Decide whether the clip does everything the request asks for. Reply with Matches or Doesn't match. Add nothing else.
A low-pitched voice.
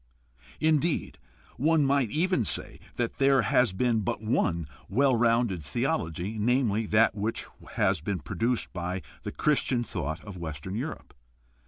Matches